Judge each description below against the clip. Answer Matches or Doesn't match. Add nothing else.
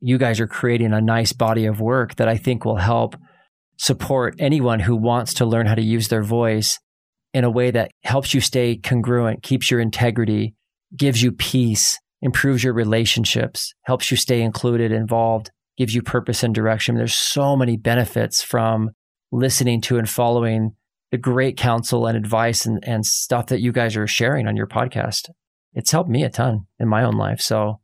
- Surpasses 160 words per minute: Matches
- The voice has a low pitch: Matches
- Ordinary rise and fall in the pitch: Doesn't match